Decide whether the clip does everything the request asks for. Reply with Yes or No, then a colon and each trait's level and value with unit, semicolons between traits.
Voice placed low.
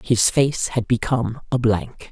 Yes: low, 120 Hz